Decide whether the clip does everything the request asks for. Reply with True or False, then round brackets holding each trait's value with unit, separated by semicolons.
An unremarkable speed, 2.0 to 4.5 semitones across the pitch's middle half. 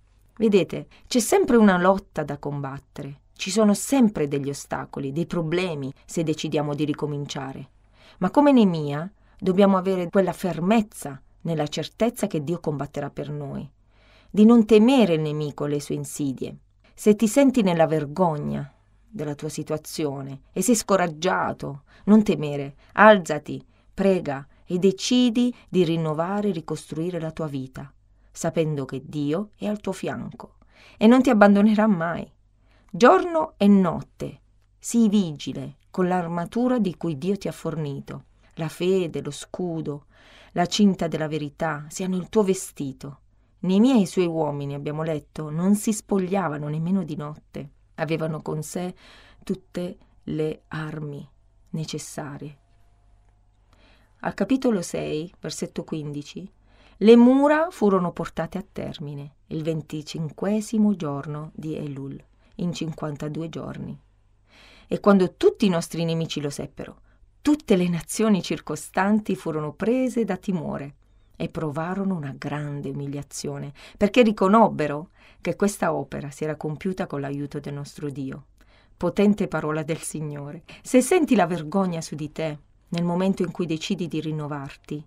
False (135 wpm; 5.2 semitones)